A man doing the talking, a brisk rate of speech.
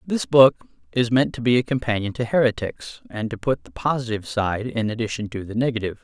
Yes: male; fast, 210 wpm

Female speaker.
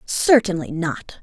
Yes: female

